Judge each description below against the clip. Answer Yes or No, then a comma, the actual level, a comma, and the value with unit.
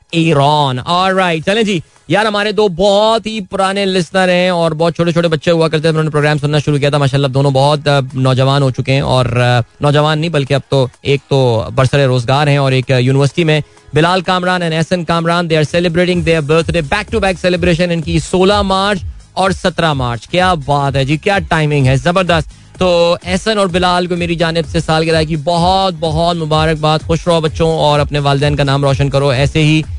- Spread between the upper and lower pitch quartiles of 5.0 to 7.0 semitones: No, average, 4.2 semitones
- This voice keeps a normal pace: No, fast, 205 wpm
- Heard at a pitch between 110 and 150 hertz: No, medium, 160 Hz